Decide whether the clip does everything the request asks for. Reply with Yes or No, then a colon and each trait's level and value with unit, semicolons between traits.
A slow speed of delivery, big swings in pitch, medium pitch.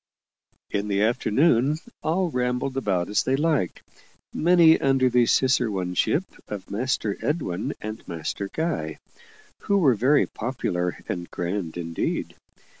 No: slow, 120 wpm; wide, 6.5 semitones; low, 120 Hz